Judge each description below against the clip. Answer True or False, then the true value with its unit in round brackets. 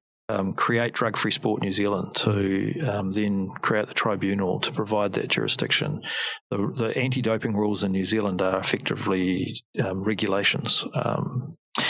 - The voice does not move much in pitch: True (1.9 semitones)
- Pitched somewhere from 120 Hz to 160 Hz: False (100 Hz)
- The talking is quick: False (150 wpm)